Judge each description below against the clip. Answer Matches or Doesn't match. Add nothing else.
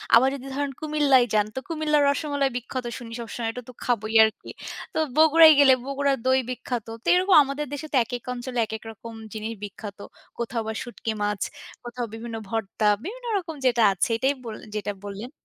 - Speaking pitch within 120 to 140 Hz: Doesn't match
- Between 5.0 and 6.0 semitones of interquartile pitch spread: Doesn't match